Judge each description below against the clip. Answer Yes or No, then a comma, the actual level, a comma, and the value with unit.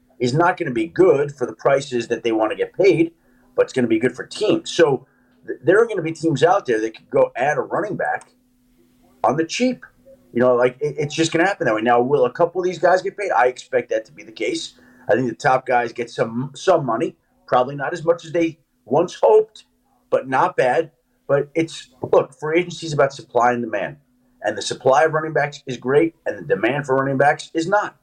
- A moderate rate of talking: No, fast, 245 wpm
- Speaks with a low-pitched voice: No, medium, 160 Hz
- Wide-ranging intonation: Yes, wide, 8.3 semitones